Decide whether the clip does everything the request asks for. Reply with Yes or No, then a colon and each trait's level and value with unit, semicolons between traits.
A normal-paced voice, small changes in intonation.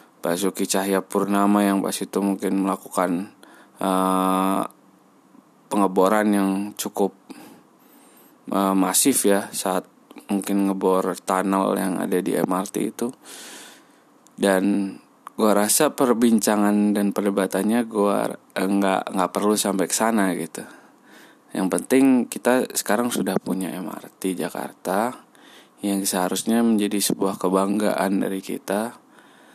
Yes: average, 110 wpm; narrow, 1.2 semitones